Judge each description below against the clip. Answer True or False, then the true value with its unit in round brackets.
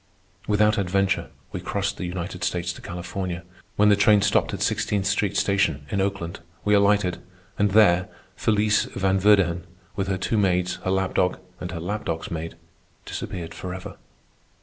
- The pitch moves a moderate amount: False (2.3 semitones)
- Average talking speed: True (165 wpm)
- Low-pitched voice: True (95 Hz)